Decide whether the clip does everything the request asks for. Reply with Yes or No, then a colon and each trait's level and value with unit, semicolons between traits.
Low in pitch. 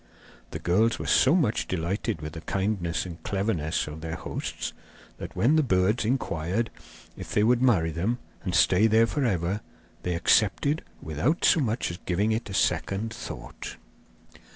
Yes: low, 100 Hz